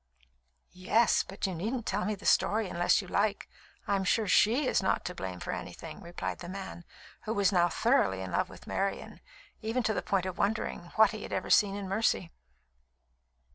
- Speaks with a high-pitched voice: Yes, high, 200 Hz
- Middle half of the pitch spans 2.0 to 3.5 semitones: Yes, average, 3.2 semitones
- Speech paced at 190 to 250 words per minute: Yes, average, 195 wpm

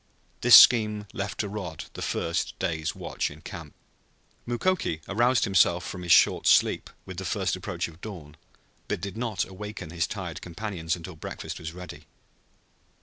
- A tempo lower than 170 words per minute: Yes, average, 160 wpm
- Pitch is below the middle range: Yes, very low, 95 Hz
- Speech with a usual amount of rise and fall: Yes, average, 4.1 semitones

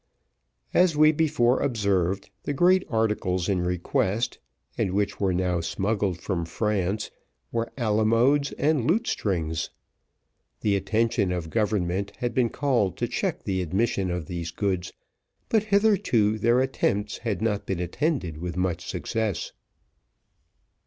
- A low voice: Yes, low, 105 Hz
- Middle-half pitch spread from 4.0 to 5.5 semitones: Yes, average, 4.8 semitones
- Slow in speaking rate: Yes, slow, 130 wpm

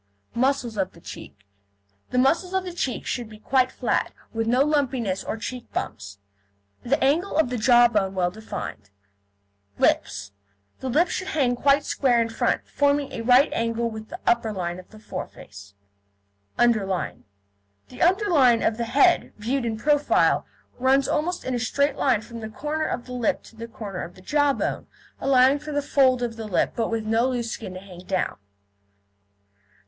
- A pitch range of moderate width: Yes, average, 4.2 semitones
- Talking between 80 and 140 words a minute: No, average, 175 wpm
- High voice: Yes, high, 240 Hz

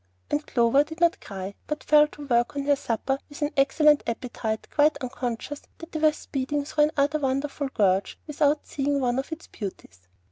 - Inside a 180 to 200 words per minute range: Yes, average, 185 wpm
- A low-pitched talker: No, very high, 280 Hz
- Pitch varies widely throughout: No, average, 3.6 semitones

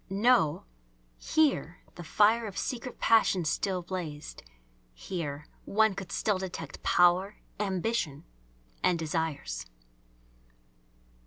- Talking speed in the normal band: No, slow, 95 wpm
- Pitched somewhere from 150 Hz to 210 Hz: Yes, medium, 185 Hz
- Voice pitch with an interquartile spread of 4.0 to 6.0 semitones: Yes, average, 4.6 semitones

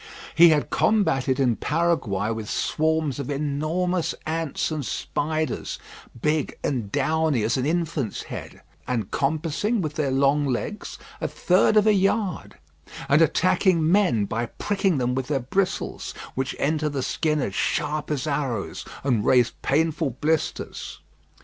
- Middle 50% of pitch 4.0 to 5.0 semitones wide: No, average, 3.6 semitones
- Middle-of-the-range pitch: Yes, medium, 150 Hz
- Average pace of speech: Yes, average, 145 wpm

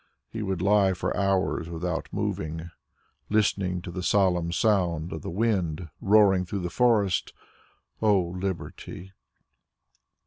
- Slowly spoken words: Yes, slow, 125 wpm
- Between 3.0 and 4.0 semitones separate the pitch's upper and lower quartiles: No, narrow, 2.6 semitones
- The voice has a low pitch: Yes, very low, 95 Hz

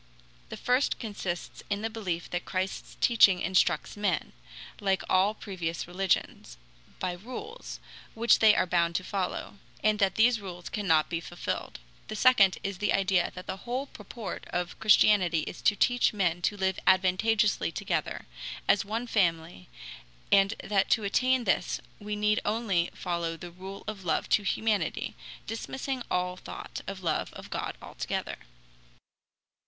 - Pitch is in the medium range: No, high, 195 Hz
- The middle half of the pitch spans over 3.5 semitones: No, average, 3.2 semitones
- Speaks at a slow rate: No, average, 150 wpm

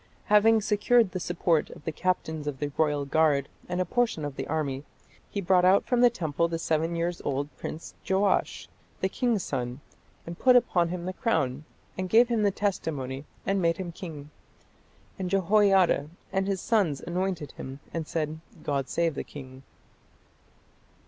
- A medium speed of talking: Yes, average, 170 wpm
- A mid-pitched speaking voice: Yes, medium, 170 Hz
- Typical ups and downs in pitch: Yes, average, 4.8 semitones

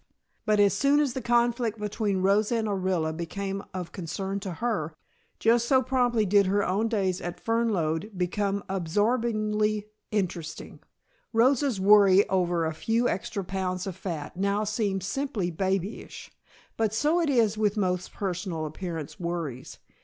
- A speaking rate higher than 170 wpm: No, average, 145 wpm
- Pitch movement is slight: No, average, 3.5 semitones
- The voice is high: Yes, high, 200 Hz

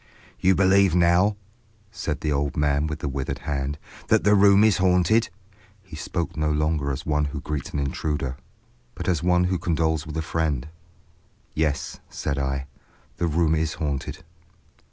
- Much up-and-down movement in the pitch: No, average, 3.5 semitones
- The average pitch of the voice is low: Yes, very low, 80 Hz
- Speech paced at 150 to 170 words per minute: Yes, average, 165 wpm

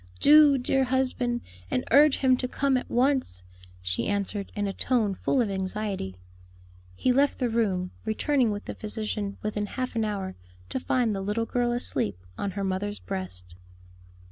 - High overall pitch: Yes, high, 215 Hz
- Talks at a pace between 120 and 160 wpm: No, average, 170 wpm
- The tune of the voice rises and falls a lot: No, average, 4.5 semitones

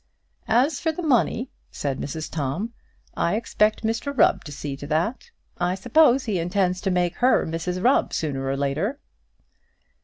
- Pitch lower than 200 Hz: Yes, medium, 185 Hz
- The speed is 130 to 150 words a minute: No, average, 160 wpm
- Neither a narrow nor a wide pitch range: No, wide, 7.2 semitones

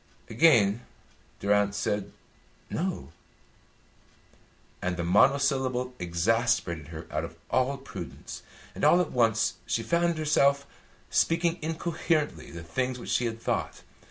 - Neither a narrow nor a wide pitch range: No, wide, 6.6 semitones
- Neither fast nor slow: No, slow, 120 wpm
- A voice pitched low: Yes, low, 125 Hz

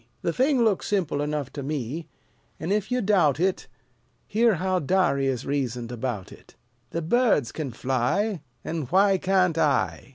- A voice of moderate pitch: Yes, medium, 165 Hz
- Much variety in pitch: Yes, wide, 6.0 semitones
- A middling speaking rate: Yes, average, 155 wpm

